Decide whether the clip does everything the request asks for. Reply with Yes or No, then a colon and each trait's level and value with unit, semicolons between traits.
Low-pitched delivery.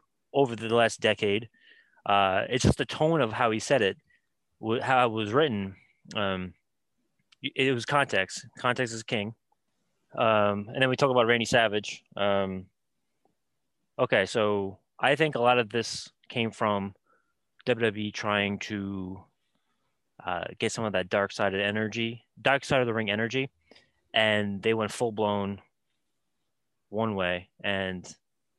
Yes: low, 110 Hz